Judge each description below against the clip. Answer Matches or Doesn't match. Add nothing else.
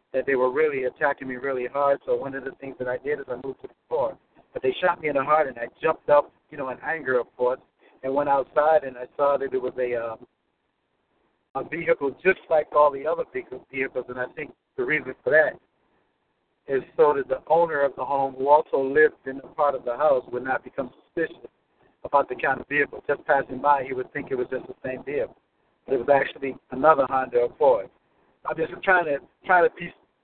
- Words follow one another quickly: Matches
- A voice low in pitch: Doesn't match